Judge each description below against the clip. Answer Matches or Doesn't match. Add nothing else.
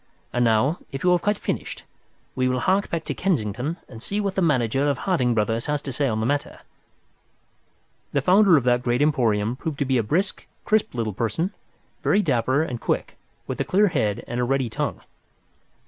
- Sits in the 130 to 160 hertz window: Matches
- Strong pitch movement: Matches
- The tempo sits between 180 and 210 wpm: Matches